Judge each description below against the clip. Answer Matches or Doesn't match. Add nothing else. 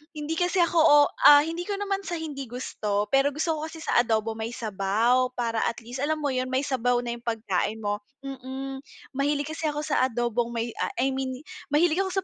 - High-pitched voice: Matches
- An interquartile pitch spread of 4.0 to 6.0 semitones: Matches